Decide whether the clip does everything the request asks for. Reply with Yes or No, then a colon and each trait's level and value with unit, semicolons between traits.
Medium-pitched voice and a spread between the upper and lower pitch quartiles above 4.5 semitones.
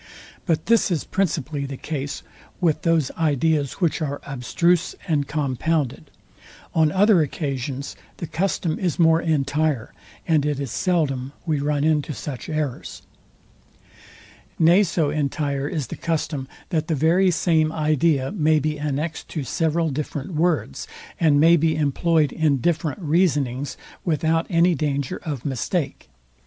No: medium, 155 Hz; average, 2.8 semitones